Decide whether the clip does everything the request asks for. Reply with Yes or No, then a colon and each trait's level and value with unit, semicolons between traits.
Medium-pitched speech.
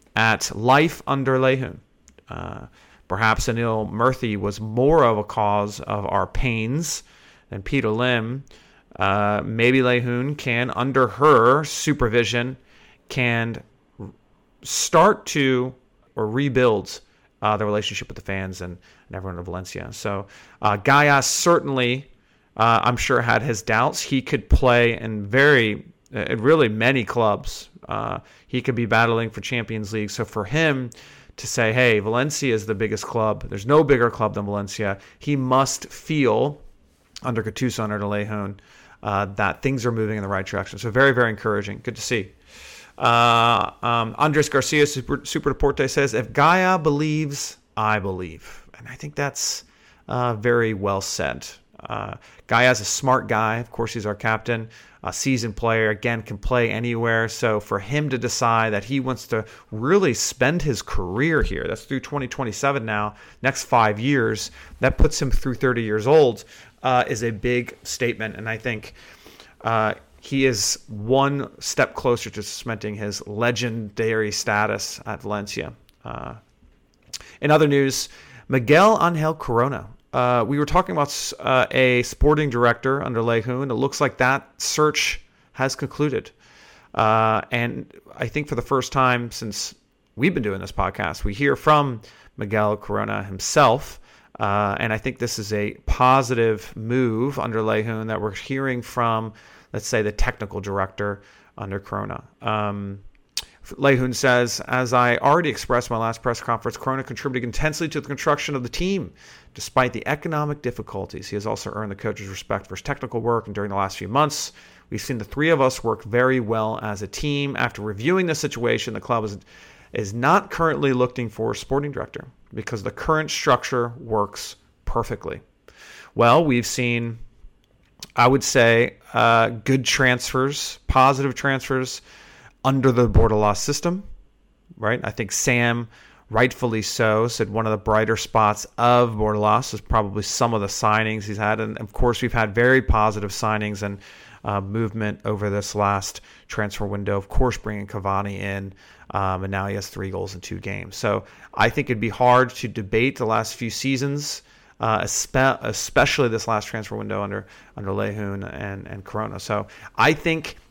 No: low, 115 Hz